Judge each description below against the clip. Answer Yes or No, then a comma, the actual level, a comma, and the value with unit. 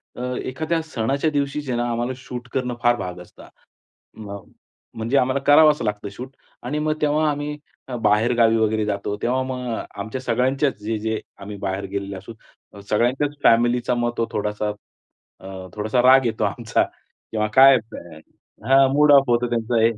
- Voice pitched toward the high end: No, low, 120 Hz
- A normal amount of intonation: Yes, average, 3.8 semitones